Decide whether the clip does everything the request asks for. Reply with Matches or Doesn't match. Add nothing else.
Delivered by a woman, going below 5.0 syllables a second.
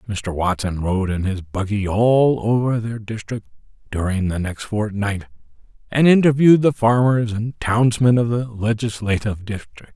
Doesn't match